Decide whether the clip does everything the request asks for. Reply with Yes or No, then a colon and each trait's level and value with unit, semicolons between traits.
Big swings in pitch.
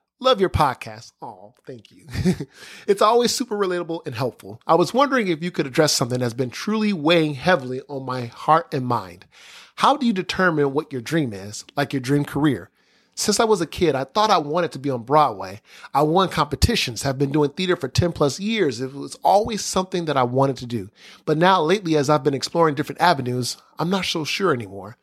Yes: wide, 5.7 semitones